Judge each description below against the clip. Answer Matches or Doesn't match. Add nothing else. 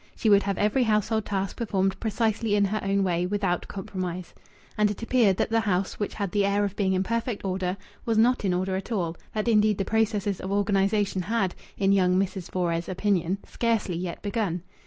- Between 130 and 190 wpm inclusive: Doesn't match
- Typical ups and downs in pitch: Doesn't match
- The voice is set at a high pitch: Matches